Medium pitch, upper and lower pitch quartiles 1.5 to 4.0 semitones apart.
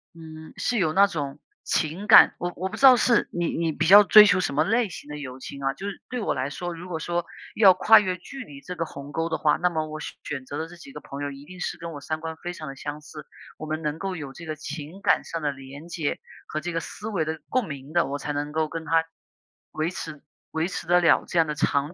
Yes: medium, 160 Hz; average, 3.3 semitones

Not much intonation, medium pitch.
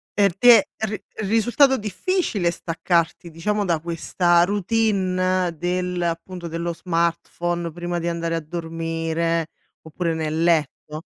Yes: narrow, 2.1 semitones; medium, 175 Hz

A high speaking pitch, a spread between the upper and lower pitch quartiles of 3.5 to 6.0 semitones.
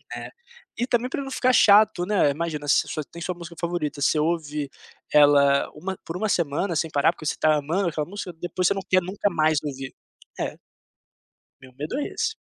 No: medium, 170 Hz; average, 4.1 semitones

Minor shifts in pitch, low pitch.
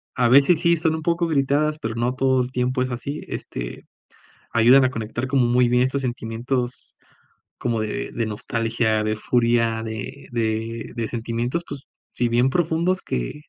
No: average, 3.2 semitones; low, 125 Hz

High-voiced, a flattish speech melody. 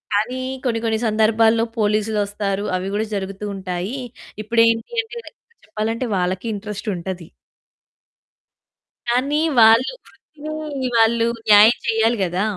Yes: high, 220 Hz; narrow, 2.3 semitones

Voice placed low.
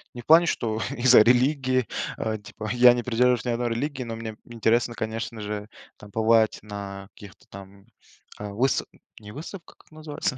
Yes: low, 115 Hz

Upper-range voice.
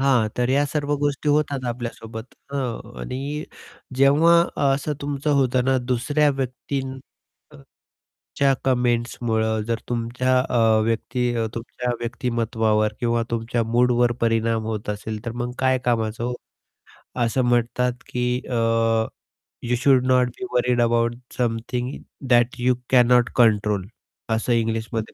No: low, 120 Hz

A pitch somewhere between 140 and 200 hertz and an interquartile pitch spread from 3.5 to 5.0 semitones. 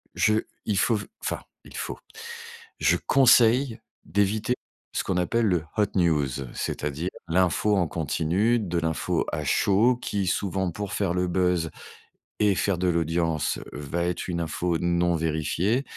No: very low, 90 Hz; average, 3.8 semitones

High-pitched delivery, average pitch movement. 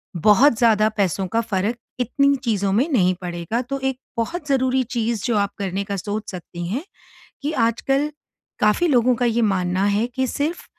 Yes: high, 230 Hz; average, 4.6 semitones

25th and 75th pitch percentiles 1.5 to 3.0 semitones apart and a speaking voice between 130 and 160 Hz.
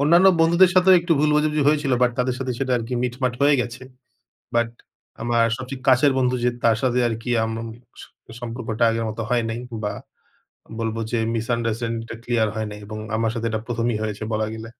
No: narrow, 2.6 semitones; low, 120 Hz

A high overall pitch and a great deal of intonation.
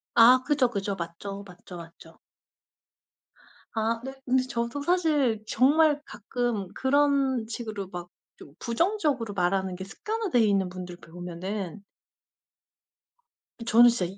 Yes: high, 225 Hz; wide, 5.7 semitones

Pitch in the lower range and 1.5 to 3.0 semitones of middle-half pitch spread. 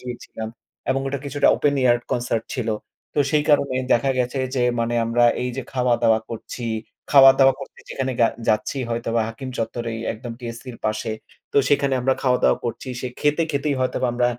Yes: low, 125 Hz; narrow, 2.5 semitones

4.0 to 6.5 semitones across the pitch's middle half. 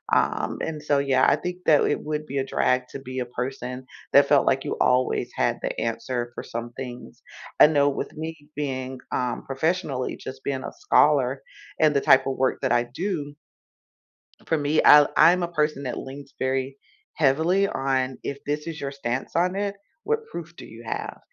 No: average, 2.8 semitones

